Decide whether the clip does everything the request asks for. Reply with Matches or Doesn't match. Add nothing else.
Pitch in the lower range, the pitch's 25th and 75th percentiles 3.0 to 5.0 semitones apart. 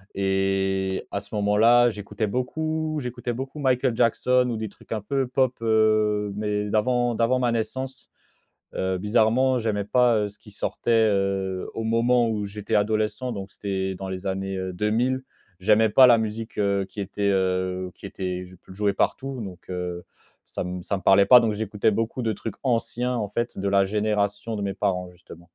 Matches